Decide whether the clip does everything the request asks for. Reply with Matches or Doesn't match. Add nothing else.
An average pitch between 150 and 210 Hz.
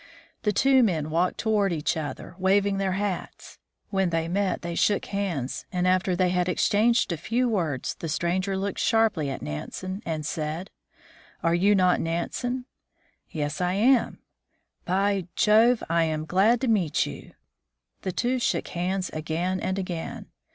Matches